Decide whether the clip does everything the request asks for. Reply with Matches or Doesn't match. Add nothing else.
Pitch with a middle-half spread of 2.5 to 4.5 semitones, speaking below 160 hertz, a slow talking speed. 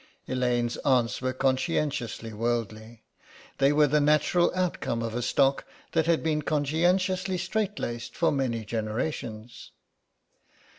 Doesn't match